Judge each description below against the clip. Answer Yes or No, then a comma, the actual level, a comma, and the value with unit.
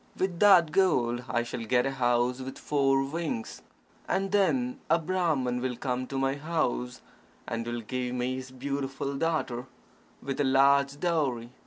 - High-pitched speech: No, low, 135 Hz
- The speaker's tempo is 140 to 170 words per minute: Yes, average, 160 wpm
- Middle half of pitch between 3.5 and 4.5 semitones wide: Yes, average, 4.2 semitones